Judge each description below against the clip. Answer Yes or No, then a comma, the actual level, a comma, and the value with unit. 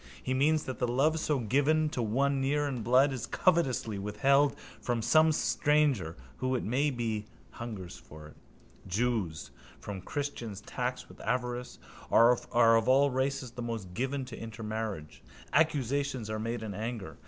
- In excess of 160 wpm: No, average, 155 wpm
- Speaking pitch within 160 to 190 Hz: No, low, 125 Hz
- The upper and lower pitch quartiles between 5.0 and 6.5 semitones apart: No, average, 4.0 semitones